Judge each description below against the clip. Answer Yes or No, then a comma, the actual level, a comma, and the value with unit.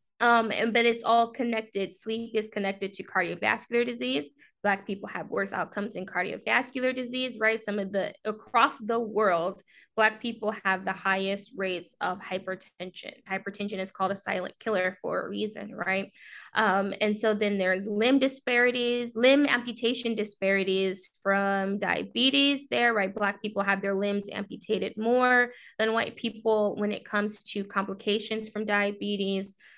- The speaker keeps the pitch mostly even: No, average, 3.0 semitones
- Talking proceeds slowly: No, average, 155 wpm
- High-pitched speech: Yes, high, 210 Hz